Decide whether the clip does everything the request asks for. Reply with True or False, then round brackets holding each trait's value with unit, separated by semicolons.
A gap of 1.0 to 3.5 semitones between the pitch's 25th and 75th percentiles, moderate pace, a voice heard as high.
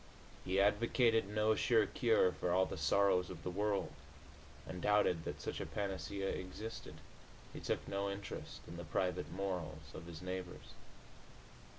False (2.4 semitones; 155 wpm; 95 Hz)